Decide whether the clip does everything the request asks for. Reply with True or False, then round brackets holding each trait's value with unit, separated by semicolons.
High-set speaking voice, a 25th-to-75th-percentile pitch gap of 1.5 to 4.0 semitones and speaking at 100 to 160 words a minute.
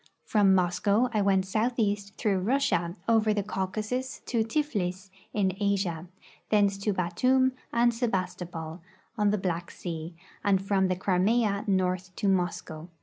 True (195 Hz; 2.9 semitones; 140 wpm)